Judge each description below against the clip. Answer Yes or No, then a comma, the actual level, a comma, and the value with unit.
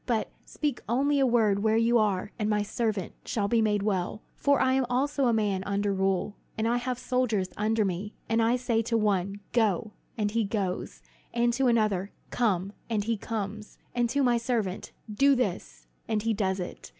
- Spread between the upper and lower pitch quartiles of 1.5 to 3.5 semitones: Yes, average, 3.0 semitones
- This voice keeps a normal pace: Yes, average, 195 wpm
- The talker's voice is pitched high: Yes, high, 220 Hz